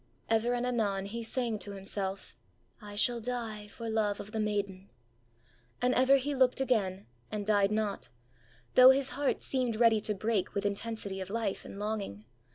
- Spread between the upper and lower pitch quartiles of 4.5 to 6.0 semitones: No, average, 3.2 semitones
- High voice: Yes, high, 215 Hz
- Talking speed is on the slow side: No, average, 170 wpm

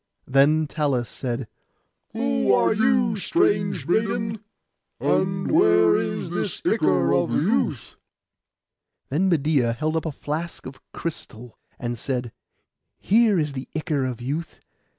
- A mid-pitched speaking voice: Yes, medium, 150 Hz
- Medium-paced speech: No, slow, 125 wpm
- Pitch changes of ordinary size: No, wide, 7.0 semitones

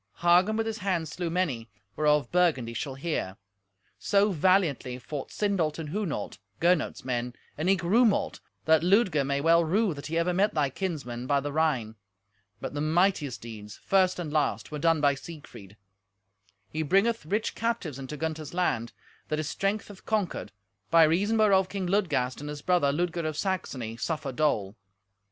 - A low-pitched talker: No, medium, 160 Hz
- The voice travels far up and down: No, average, 4.8 semitones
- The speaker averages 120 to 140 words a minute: No, average, 170 wpm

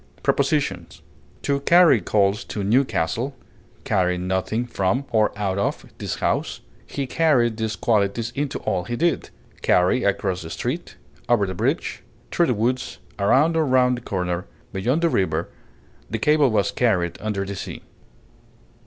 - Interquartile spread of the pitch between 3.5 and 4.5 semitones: No, average, 5.1 semitones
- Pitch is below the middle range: Yes, low, 110 Hz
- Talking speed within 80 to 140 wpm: No, average, 150 wpm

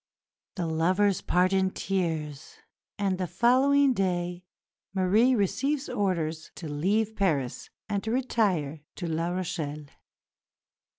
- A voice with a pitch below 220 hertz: Yes, medium, 185 Hz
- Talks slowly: Yes, slow, 115 wpm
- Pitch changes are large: No, average, 4.2 semitones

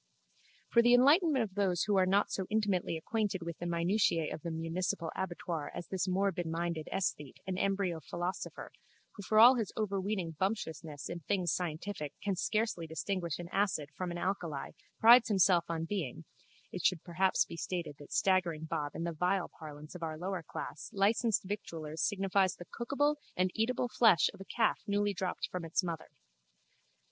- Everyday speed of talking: Yes, average, 170 wpm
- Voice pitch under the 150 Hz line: No, medium, 185 Hz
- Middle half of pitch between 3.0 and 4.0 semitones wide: Yes, average, 3.5 semitones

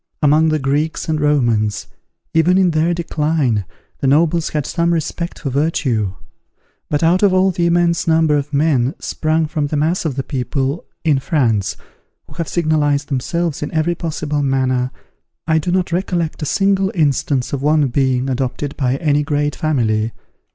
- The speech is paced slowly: No, average, 165 wpm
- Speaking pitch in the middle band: Yes, medium, 150 Hz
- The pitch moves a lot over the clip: No, average, 3.5 semitones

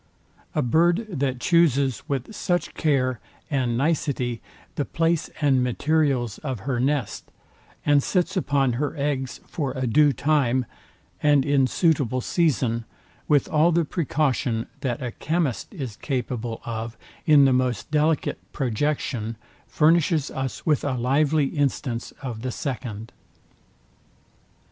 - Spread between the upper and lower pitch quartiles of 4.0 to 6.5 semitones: No, average, 3.5 semitones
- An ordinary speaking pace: No, slow, 130 wpm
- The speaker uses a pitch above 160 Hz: No, low, 135 Hz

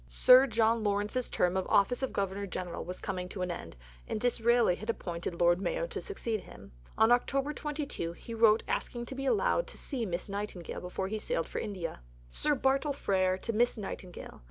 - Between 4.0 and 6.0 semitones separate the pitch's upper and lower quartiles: Yes, average, 5.1 semitones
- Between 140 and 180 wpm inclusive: No, average, 195 wpm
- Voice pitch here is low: No, high, 215 Hz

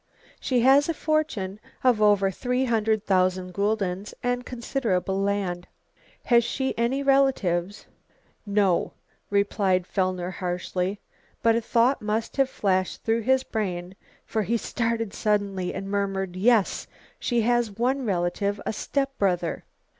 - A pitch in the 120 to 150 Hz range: No, high, 210 Hz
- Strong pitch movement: No, average, 4.2 semitones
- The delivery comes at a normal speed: No, slow, 130 wpm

